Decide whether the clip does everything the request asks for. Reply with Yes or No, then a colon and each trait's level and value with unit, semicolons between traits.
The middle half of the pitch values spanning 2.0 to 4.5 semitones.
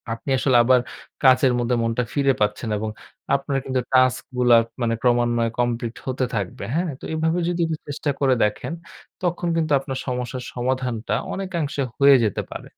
Yes: average, 2.9 semitones